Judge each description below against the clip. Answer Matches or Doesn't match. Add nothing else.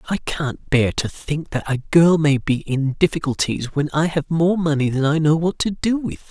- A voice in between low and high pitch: Matches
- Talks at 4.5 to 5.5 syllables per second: Matches